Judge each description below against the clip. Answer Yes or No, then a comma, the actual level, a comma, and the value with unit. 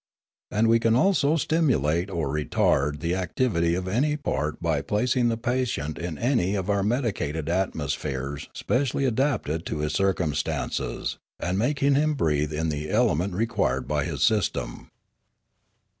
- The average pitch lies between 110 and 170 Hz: No, very low, 95 Hz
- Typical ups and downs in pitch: No, wide, 7.9 semitones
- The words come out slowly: No, average, 145 wpm